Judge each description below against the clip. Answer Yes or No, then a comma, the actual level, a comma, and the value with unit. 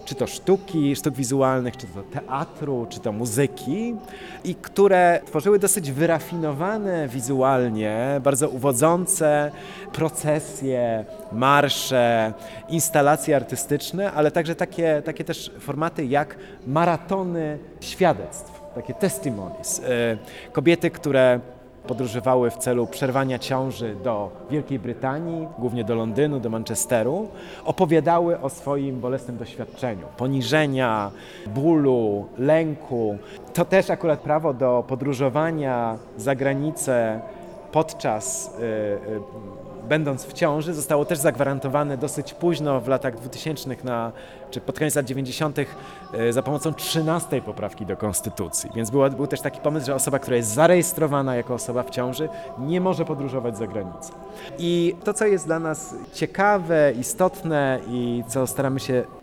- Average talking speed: Yes, average, 125 wpm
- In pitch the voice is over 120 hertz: Yes, medium, 140 Hz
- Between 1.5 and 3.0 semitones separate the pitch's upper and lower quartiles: No, average, 4.6 semitones